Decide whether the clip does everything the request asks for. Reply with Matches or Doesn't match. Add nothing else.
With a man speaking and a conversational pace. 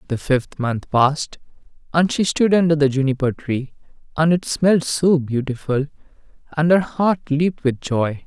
Matches